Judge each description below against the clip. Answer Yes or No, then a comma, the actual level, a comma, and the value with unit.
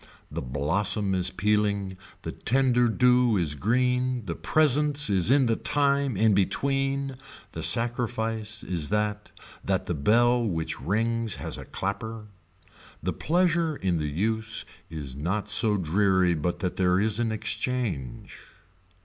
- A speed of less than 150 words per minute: Yes, average, 140 wpm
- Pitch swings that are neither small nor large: Yes, average, 4.9 semitones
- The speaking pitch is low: Yes, low, 105 Hz